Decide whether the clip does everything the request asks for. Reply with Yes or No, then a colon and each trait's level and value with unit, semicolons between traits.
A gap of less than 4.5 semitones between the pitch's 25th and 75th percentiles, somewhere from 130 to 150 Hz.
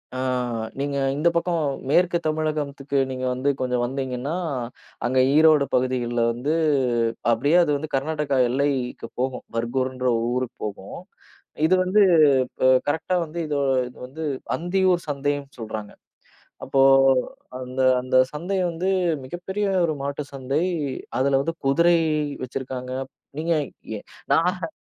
Yes: average, 4.1 semitones; medium, 140 Hz